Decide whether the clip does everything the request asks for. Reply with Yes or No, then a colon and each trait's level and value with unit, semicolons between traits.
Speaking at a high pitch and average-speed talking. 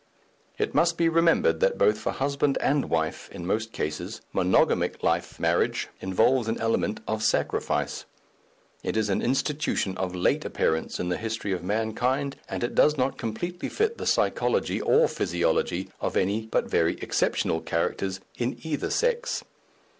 No: low, 120 Hz; average, 155 wpm